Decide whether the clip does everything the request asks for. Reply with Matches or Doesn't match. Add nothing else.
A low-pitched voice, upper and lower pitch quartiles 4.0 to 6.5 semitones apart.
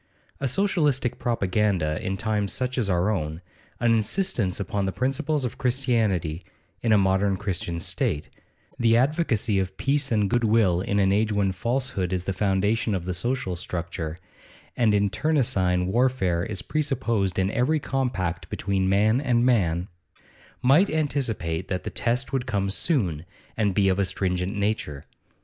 Matches